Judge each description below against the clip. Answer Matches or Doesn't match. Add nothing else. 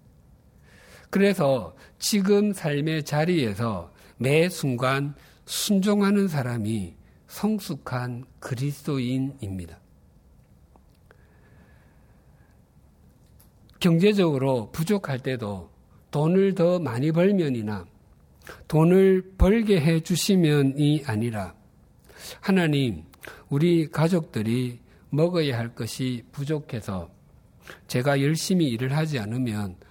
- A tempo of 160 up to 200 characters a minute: Matches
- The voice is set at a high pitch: Doesn't match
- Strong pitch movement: Matches